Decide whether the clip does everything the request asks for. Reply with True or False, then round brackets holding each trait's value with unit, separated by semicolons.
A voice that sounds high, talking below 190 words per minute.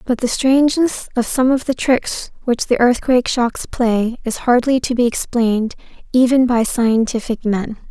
True (245 Hz; 165 wpm)